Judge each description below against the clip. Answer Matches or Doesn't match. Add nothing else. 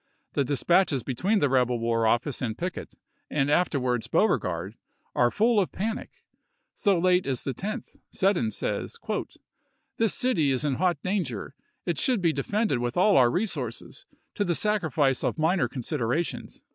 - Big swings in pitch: Matches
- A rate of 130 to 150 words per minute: Doesn't match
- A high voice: Doesn't match